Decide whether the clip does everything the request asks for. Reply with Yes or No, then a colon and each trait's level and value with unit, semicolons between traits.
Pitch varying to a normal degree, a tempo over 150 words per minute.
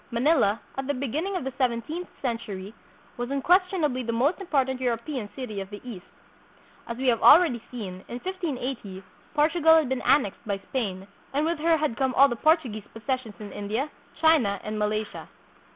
No: wide, 5.7 semitones; average, 175 wpm